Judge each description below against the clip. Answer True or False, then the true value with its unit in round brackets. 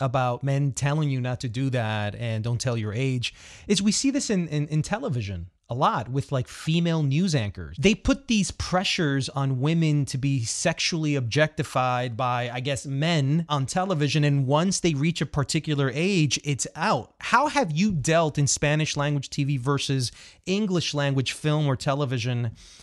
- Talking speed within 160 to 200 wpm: True (175 wpm)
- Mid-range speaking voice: True (145 Hz)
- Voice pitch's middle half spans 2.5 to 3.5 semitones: False (4.2 semitones)